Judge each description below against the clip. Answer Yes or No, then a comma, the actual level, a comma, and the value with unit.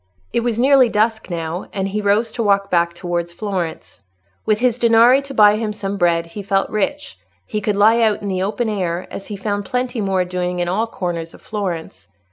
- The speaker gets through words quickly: Yes, fast, 210 wpm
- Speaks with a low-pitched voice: No, high, 205 Hz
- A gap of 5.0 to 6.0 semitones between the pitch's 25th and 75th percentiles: No, average, 3.7 semitones